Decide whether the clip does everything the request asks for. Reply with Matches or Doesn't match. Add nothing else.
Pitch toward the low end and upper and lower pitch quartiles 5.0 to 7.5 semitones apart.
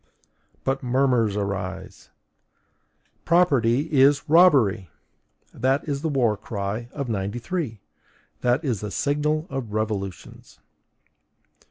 Matches